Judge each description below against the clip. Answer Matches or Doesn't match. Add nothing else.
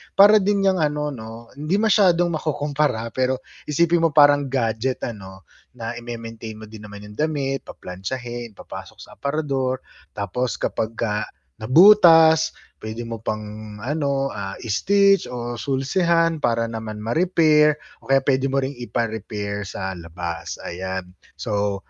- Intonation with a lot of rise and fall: Matches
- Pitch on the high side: Doesn't match